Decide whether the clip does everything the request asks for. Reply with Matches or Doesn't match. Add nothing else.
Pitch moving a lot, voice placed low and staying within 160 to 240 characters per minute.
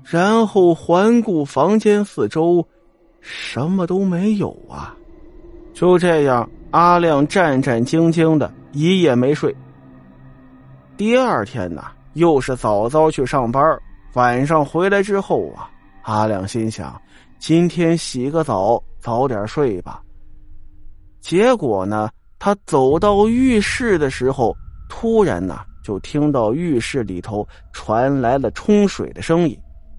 Doesn't match